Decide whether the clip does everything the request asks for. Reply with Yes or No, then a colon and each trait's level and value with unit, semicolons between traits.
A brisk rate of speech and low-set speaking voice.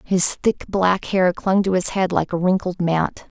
No: fast, 215 wpm; medium, 185 Hz